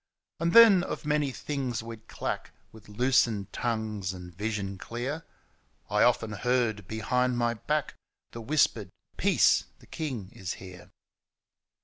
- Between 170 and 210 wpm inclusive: No, average, 140 wpm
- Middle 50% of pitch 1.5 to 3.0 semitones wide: No, average, 4.3 semitones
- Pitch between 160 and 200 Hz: No, low, 115 Hz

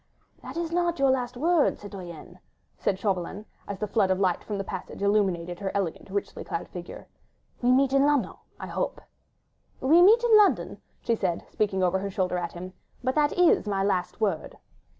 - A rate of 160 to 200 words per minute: Yes, average, 190 wpm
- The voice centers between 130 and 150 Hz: No, high, 200 Hz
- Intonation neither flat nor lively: No, wide, 6.6 semitones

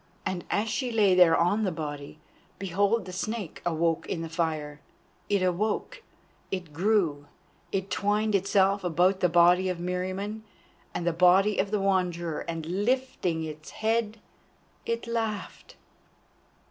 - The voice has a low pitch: No, medium, 185 Hz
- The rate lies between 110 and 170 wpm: Yes, average, 140 wpm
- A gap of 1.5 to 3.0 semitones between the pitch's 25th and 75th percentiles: No, average, 3.5 semitones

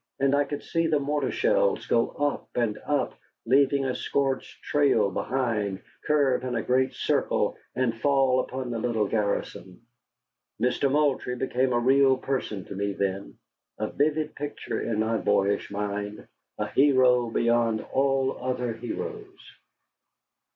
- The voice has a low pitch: Yes, low, 130 Hz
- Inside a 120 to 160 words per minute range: Yes, average, 145 wpm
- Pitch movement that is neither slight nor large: Yes, average, 3.8 semitones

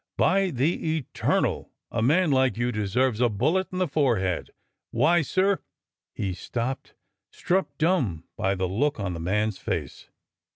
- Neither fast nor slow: Yes, average, 150 wpm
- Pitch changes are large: Yes, wide, 8.2 semitones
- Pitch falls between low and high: No, low, 125 Hz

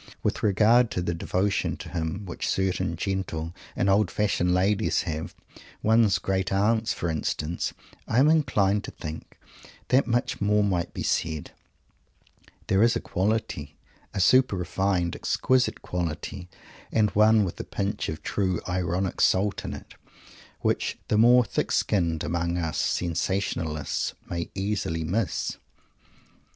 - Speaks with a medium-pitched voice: No, very low, 95 Hz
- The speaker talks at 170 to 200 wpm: No, average, 140 wpm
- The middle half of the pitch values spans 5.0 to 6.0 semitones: No, average, 3.6 semitones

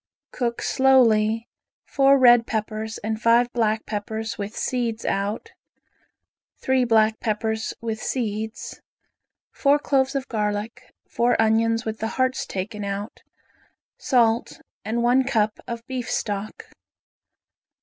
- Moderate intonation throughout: No, narrow, 2.1 semitones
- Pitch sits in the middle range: No, high, 225 Hz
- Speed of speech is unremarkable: No, slow, 120 wpm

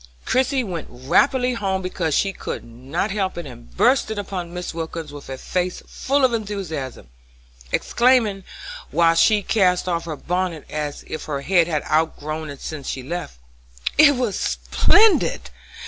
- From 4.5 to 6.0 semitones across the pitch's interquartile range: Yes, average, 5.2 semitones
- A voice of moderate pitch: Yes, medium, 175 Hz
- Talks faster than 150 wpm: Yes, average, 160 wpm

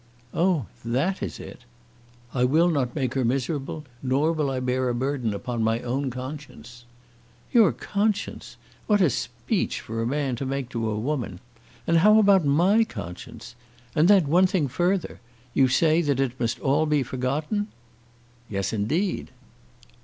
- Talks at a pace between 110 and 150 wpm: No, average, 160 wpm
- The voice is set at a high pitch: No, medium, 140 Hz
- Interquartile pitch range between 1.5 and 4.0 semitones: No, average, 5.2 semitones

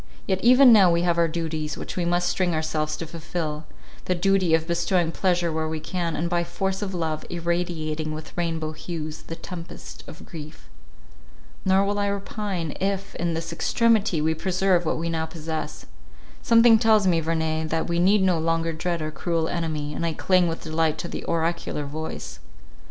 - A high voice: No, medium, 170 Hz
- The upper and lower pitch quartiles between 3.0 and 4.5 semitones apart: No, narrow, 2.5 semitones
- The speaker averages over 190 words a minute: No, average, 185 wpm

